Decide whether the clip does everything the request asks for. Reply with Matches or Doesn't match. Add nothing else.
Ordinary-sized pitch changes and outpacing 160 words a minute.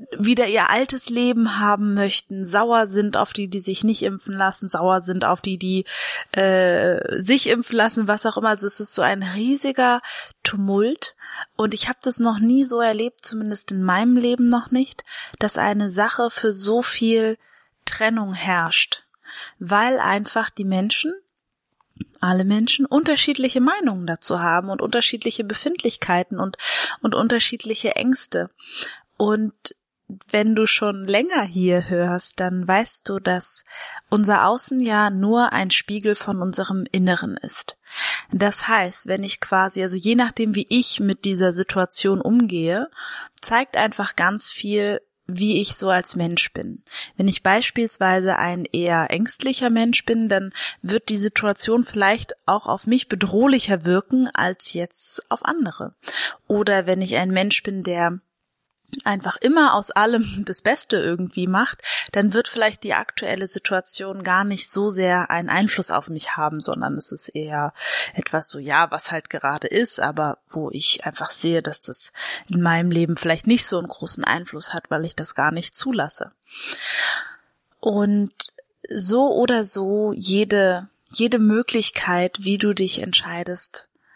Doesn't match